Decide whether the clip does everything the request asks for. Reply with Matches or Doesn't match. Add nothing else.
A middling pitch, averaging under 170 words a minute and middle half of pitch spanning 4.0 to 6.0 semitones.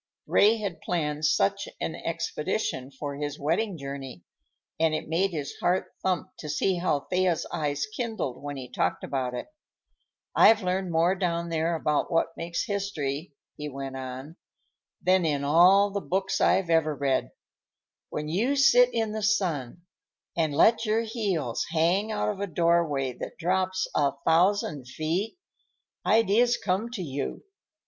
Matches